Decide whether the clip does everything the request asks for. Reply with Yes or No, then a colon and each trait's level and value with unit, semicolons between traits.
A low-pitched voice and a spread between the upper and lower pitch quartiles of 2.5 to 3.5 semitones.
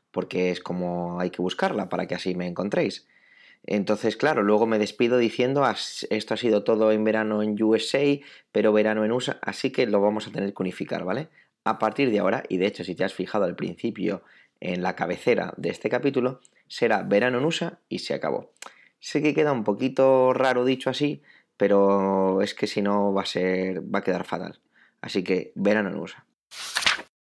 No: low, 105 Hz; average, 4.3 semitones